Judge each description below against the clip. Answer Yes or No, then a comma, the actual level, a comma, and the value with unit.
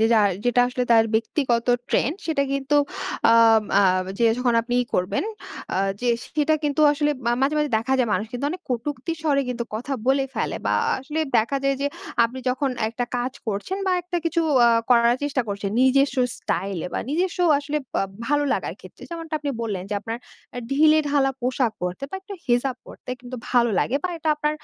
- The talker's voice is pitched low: No, very high, 265 Hz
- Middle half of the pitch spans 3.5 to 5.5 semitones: Yes, average, 4.0 semitones